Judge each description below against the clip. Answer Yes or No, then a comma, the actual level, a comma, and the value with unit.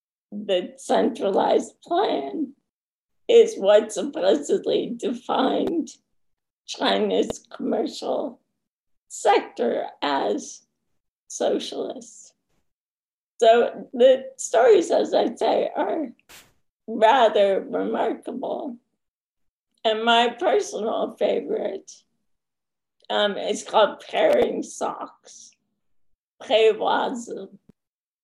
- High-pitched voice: Yes, very high, 250 Hz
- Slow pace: Yes, slow, 65 wpm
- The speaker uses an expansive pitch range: Yes, wide, 8.6 semitones